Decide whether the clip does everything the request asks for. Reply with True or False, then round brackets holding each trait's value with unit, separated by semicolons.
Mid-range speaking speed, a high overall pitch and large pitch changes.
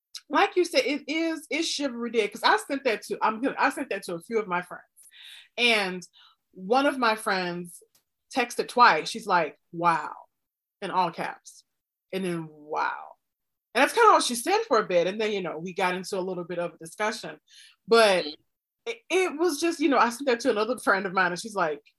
False (220 wpm; 220 Hz; 7.7 semitones)